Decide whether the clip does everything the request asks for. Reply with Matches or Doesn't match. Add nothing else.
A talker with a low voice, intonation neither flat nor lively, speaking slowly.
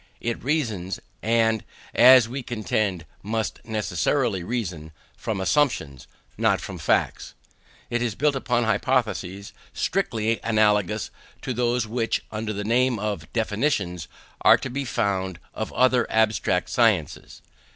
Matches